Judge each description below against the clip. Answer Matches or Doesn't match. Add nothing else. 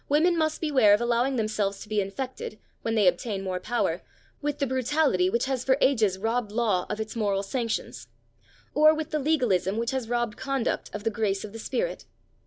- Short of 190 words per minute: Doesn't match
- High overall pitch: Matches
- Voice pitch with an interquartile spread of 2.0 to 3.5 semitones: Doesn't match